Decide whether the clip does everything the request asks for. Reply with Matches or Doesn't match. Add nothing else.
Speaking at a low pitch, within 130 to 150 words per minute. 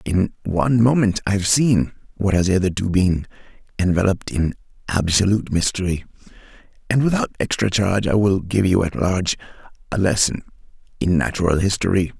Matches